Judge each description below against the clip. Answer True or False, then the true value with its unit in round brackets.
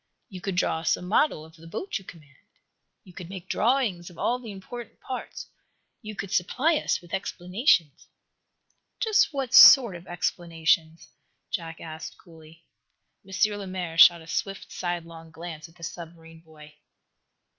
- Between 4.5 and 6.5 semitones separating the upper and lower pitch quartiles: False (3.3 semitones)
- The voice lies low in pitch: False (175 Hz)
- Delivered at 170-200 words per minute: False (155 wpm)